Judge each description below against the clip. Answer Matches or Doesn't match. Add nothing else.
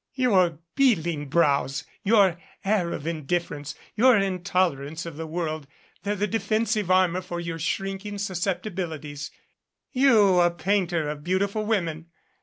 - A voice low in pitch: Doesn't match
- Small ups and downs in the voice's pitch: Doesn't match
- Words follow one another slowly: Matches